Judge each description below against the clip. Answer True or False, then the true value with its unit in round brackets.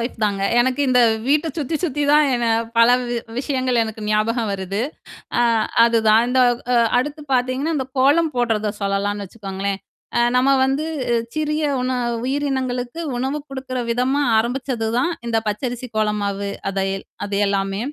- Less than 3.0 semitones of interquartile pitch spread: False (4.0 semitones)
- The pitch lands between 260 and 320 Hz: False (245 Hz)